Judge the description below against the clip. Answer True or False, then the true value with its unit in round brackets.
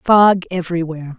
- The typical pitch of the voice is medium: True (175 Hz)